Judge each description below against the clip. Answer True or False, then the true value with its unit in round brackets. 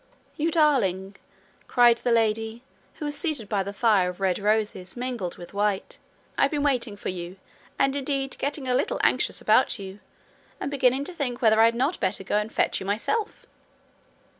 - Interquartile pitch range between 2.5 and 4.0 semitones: False (5.4 semitones)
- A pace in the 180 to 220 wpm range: True (185 wpm)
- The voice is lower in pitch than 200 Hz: False (230 Hz)